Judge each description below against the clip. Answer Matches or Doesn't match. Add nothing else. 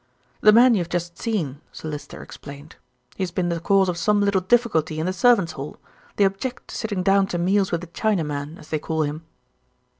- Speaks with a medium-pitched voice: Matches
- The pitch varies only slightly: Doesn't match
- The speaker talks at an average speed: Doesn't match